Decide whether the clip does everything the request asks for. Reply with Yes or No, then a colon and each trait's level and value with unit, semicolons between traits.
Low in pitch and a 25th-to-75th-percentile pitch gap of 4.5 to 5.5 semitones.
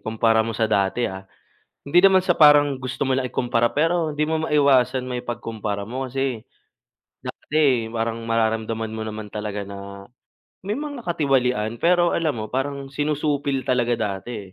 Yes: low, 125 Hz; average, 4.8 semitones